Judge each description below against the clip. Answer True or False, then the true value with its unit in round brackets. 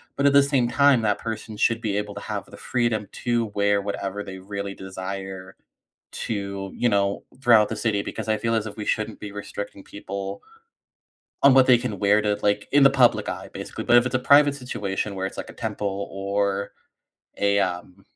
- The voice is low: True (105 Hz)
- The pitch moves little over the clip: False (3.1 semitones)